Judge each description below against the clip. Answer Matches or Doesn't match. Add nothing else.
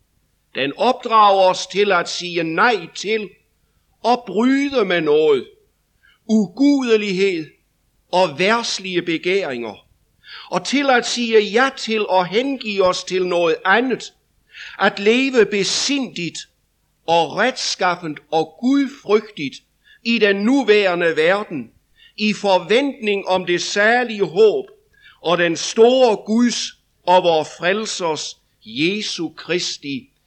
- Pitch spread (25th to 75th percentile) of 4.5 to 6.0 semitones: Matches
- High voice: Matches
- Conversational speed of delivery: Doesn't match